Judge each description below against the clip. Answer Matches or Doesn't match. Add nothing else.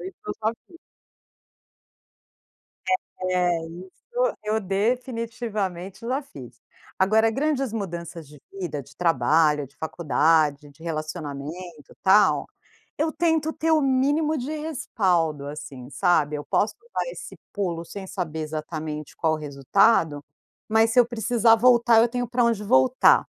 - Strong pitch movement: Matches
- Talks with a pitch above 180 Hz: Matches